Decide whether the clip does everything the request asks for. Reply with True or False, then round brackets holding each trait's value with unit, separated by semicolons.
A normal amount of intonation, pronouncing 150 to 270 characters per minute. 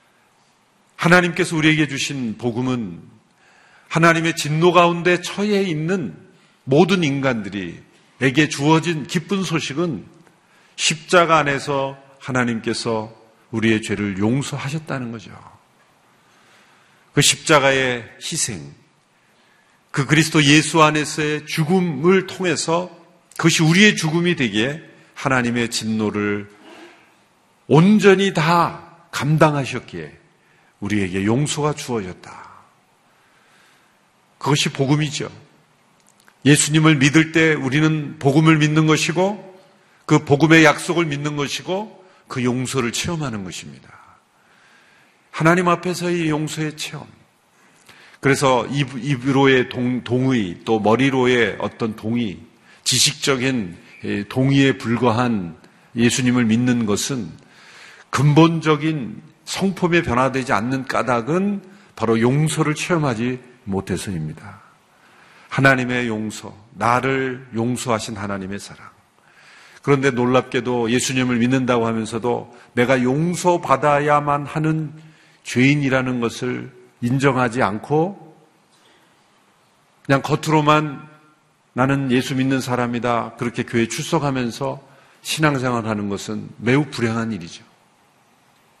True (4.9 semitones; 245 characters per minute)